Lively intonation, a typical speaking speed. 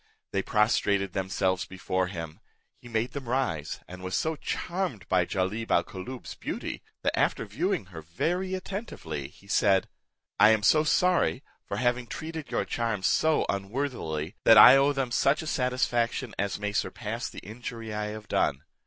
Yes: wide, 6.1 semitones; average, 165 wpm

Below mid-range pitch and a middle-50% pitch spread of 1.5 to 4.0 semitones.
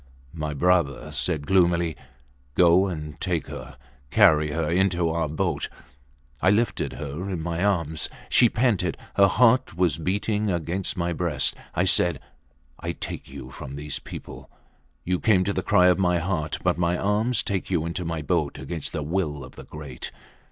Yes: very low, 85 Hz; average, 3.6 semitones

